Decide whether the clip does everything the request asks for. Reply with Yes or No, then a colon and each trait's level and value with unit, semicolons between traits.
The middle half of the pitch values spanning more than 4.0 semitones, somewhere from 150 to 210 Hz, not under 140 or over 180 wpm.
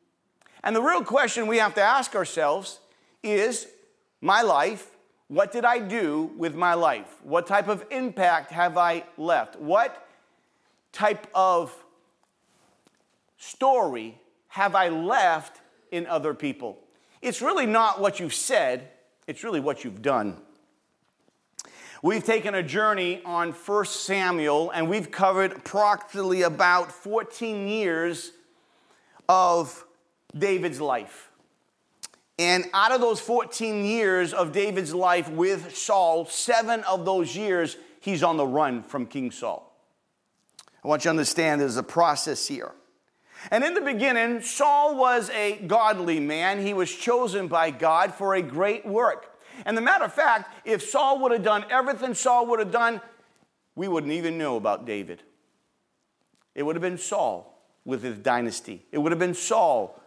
Yes: average, 5.1 semitones; high, 190 Hz; average, 145 wpm